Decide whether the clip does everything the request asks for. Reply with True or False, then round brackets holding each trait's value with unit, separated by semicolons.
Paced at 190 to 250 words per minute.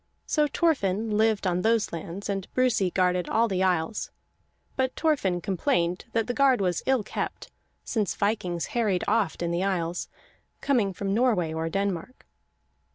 False (155 wpm)